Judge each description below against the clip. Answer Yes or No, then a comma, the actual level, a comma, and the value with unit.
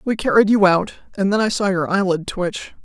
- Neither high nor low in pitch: No, high, 195 Hz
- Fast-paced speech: Yes, fast, 230 wpm